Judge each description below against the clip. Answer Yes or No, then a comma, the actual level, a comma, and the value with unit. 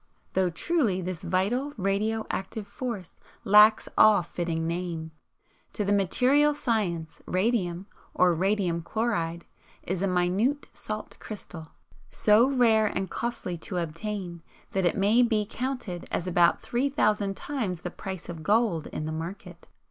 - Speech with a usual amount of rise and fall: Yes, average, 4.1 semitones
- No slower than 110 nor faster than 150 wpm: Yes, average, 140 wpm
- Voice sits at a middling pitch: No, high, 195 Hz